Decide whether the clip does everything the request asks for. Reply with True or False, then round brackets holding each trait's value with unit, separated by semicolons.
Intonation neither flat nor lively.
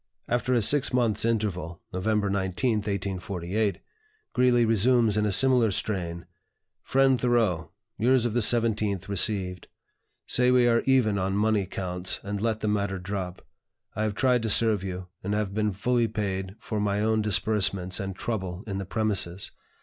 True (3.2 semitones)